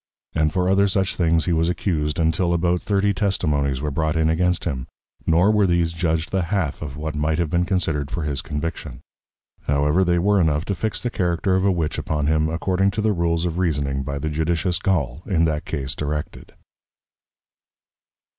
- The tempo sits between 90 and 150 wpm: No, average, 195 wpm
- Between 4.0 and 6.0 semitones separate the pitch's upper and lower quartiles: No, average, 3.2 semitones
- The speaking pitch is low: Yes, very low, 85 Hz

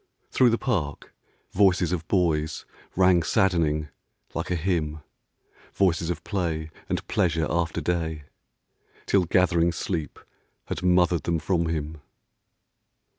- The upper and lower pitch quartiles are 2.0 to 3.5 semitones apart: Yes, narrow, 2.4 semitones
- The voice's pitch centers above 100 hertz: No, very low, 85 Hz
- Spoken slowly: Yes, slow, 120 wpm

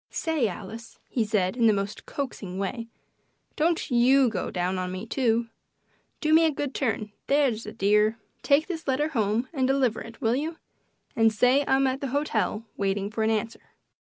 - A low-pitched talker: No, high, 230 Hz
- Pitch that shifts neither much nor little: Yes, average, 4.6 semitones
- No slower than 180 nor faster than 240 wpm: Yes, average, 185 wpm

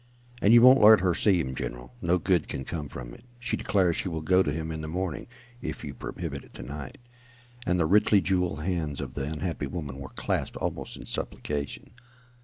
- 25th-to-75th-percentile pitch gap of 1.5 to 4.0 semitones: No, average, 4.4 semitones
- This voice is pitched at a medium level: No, very low, 80 Hz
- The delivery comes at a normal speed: No, fast, 210 wpm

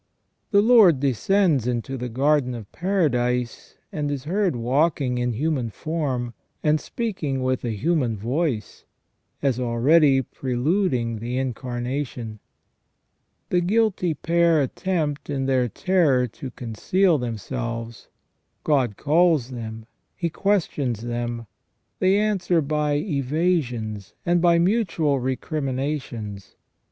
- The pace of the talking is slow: Yes, slow, 110 wpm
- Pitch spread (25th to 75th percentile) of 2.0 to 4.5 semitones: No, wide, 5.6 semitones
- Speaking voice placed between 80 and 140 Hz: Yes, low, 135 Hz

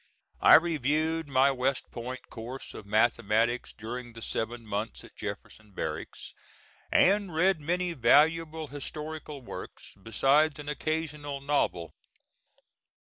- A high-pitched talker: No, medium, 140 Hz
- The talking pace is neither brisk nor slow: No, slow, 115 wpm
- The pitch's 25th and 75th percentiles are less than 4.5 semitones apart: No, average, 5.0 semitones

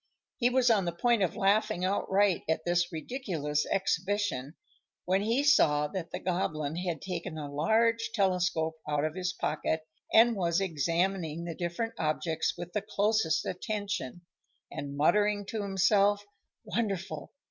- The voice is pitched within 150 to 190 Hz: Yes, medium, 185 Hz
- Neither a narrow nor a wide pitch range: Yes, average, 4.2 semitones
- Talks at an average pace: Yes, average, 145 wpm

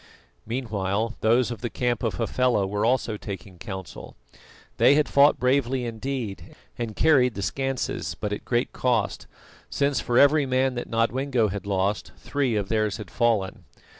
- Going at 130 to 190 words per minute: Yes, average, 160 wpm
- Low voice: Yes, low, 120 Hz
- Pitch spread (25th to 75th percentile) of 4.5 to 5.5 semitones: No, average, 3.9 semitones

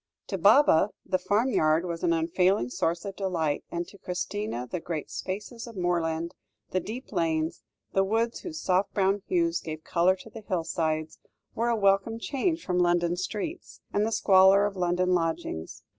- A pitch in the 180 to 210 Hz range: Yes, medium, 185 Hz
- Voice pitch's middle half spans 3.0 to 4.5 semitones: Yes, average, 3.7 semitones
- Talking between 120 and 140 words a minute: No, average, 170 wpm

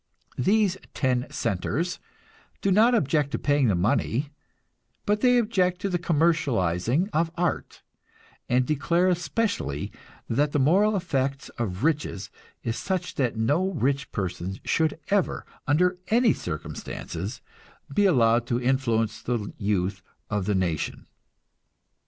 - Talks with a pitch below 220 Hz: Yes, medium, 140 Hz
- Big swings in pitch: Yes, wide, 8.0 semitones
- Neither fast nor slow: No, slow, 130 wpm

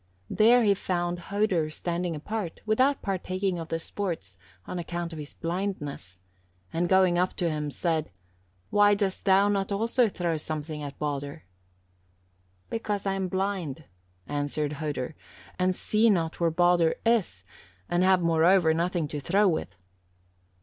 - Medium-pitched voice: Yes, medium, 175 Hz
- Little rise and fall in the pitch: No, average, 3.7 semitones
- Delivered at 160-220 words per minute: No, average, 145 wpm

